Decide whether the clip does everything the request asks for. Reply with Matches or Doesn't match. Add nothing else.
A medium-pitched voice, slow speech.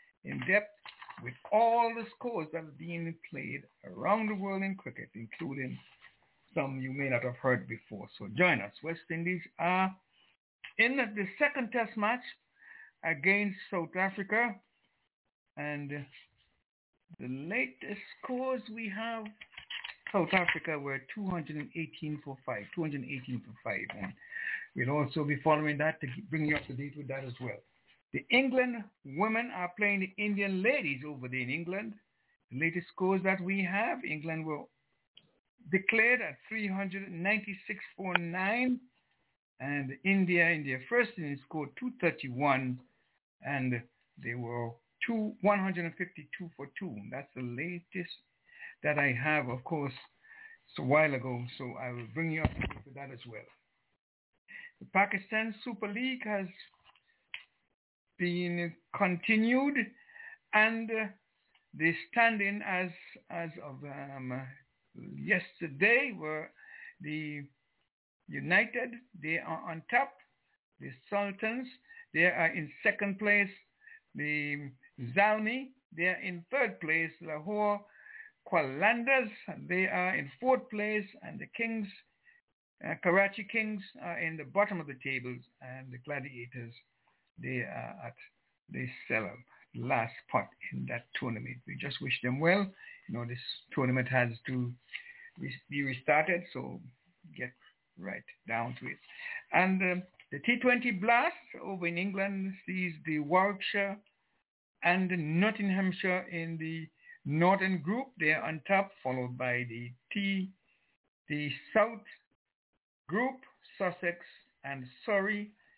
Matches